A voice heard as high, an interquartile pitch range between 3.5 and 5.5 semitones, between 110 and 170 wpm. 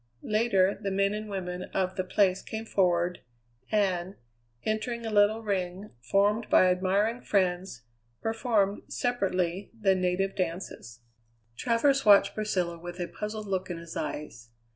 No: high, 195 Hz; average, 2.8 semitones; average, 140 wpm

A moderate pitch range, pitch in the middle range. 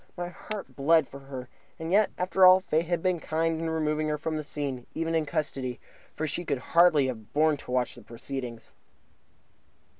Yes: average, 3.4 semitones; medium, 155 Hz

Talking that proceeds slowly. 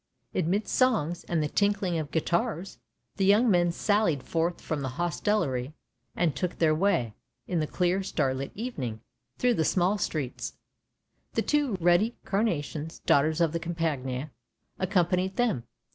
No: average, 145 wpm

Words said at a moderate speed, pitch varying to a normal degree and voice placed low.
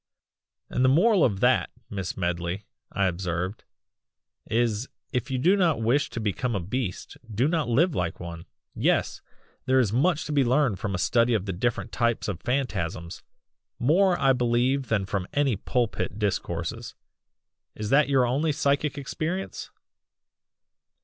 No: average, 155 wpm; wide, 5.9 semitones; low, 120 Hz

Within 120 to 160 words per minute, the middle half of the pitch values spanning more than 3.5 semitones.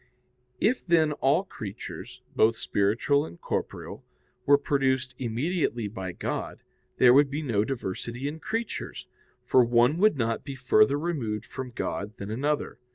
Yes: average, 145 wpm; average, 4.5 semitones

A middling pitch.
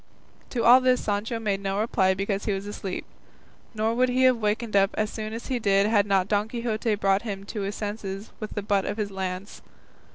No: high, 210 Hz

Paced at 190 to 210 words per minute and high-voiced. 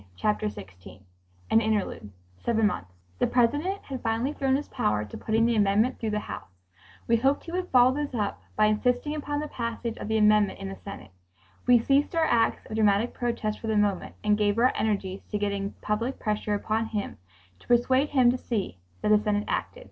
Yes: average, 200 wpm; high, 220 Hz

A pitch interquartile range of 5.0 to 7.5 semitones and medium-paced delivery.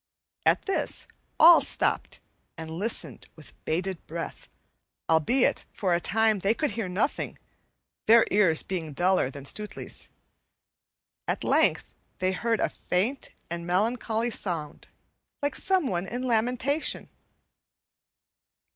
No: wide, 5.4 semitones; slow, 115 wpm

